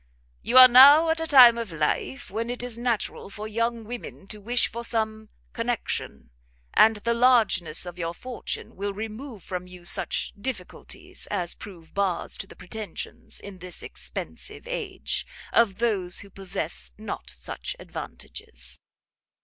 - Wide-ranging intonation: No, average, 4.7 semitones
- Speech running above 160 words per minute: No, average, 150 wpm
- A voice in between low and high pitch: No, high, 215 Hz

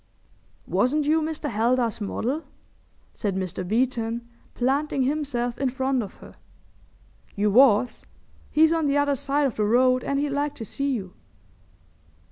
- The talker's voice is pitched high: Yes, very high, 260 Hz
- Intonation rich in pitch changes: No, average, 3.9 semitones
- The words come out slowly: No, average, 145 wpm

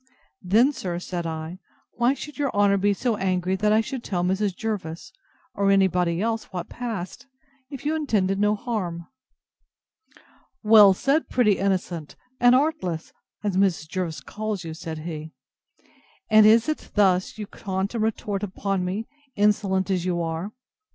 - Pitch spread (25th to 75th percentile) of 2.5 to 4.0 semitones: Yes, average, 3.4 semitones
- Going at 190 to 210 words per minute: No, average, 155 wpm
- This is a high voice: Yes, high, 195 Hz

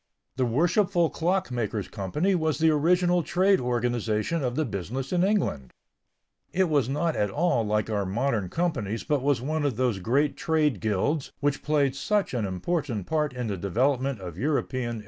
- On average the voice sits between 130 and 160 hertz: Yes, low, 135 Hz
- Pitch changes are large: Yes, wide, 6.2 semitones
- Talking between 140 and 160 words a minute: No, average, 175 wpm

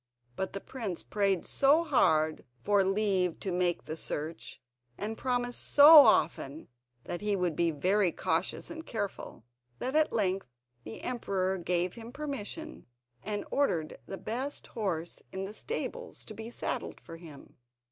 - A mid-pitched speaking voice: No, high, 195 Hz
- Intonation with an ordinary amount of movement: No, wide, 5.9 semitones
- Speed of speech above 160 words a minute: No, average, 150 wpm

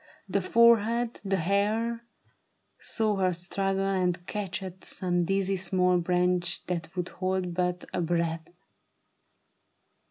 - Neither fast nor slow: No, slow, 125 wpm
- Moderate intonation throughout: No, narrow, 2.0 semitones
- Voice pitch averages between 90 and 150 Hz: No, medium, 185 Hz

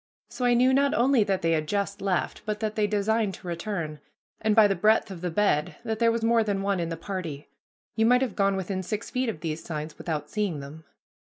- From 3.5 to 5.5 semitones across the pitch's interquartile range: Yes, average, 4.7 semitones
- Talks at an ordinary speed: No, fast, 235 wpm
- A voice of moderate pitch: No, high, 200 Hz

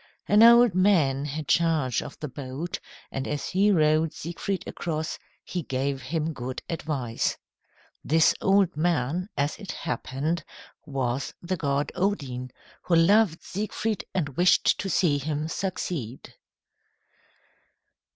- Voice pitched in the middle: Yes, medium, 160 Hz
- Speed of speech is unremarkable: No, slow, 125 wpm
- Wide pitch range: No, average, 4.7 semitones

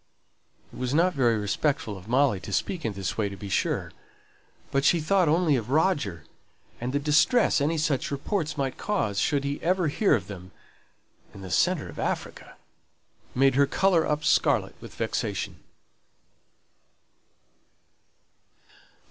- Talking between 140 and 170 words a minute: Yes, average, 150 wpm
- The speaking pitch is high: No, medium, 140 Hz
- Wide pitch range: Yes, wide, 6.5 semitones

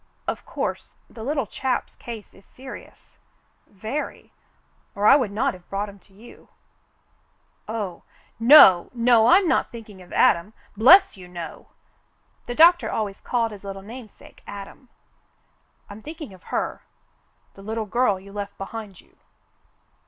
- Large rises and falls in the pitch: No, average, 3.7 semitones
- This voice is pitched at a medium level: No, high, 215 Hz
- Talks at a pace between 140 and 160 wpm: Yes, average, 150 wpm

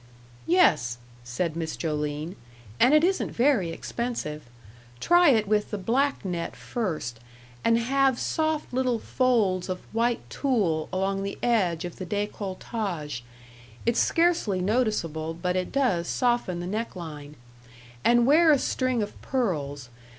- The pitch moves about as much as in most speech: No, wide, 6.7 semitones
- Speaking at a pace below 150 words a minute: Yes, slow, 135 wpm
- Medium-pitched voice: No, high, 205 Hz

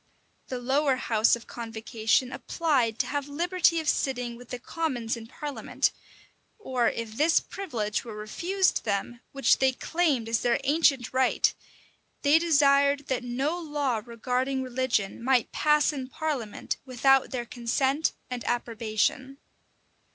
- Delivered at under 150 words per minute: Yes, average, 140 wpm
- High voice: Yes, very high, 260 Hz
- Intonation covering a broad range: No, average, 3.6 semitones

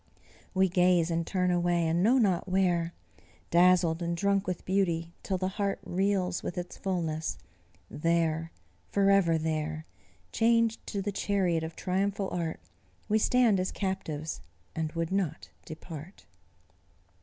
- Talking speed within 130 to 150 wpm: Yes, slow, 135 wpm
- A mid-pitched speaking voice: Yes, medium, 180 Hz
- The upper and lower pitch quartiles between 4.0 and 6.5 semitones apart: No, average, 2.9 semitones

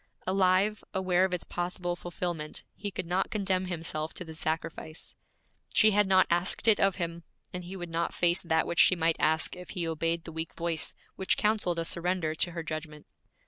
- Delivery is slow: No, average, 195 wpm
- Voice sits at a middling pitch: Yes, medium, 175 Hz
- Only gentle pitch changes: Yes, narrow, 2.2 semitones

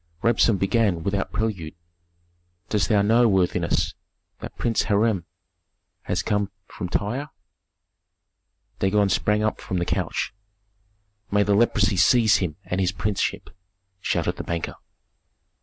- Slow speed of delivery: Yes, slow, 125 wpm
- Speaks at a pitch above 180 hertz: No, low, 100 Hz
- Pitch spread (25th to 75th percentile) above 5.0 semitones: No, narrow, 2.6 semitones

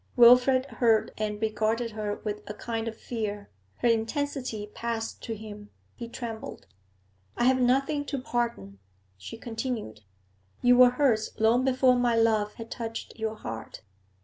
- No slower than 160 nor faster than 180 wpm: No, average, 150 wpm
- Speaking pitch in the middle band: No, high, 230 Hz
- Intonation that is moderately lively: No, narrow, 2.3 semitones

